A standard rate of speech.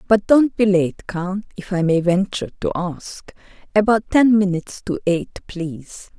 Yes: average, 165 wpm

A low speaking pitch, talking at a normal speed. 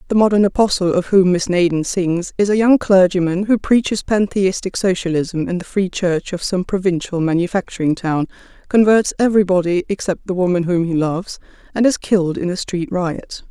No: medium, 185 Hz; average, 180 wpm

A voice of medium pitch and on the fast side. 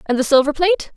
No: very high, 305 Hz; fast, 250 wpm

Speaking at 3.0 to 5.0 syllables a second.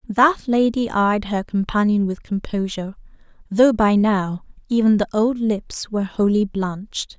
Yes: 4.4 syllables/s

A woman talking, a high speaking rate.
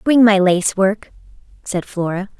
No: female; average, 150 wpm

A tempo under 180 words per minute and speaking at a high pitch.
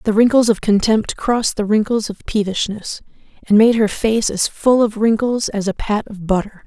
No: average, 200 wpm; high, 215 Hz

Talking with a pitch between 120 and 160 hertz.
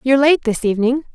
No: very high, 255 Hz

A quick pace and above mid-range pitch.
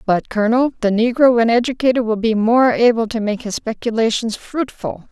No: average, 175 wpm; high, 230 Hz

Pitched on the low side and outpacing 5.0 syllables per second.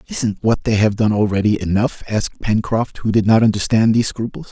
Yes: low, 110 Hz; 5.5 syllables/s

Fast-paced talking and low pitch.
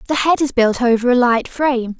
No: fast, 240 wpm; very high, 250 Hz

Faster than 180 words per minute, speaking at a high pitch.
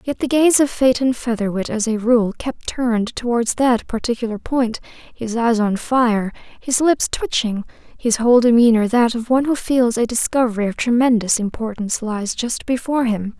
No: average, 175 wpm; high, 235 Hz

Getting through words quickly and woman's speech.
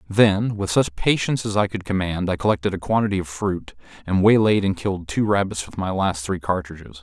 No: fast, 215 wpm; male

